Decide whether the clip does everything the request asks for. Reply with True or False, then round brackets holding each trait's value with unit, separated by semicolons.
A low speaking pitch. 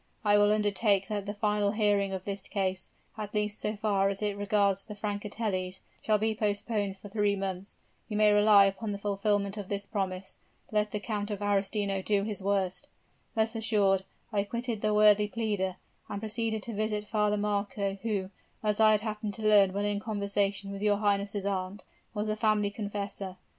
False (205 Hz)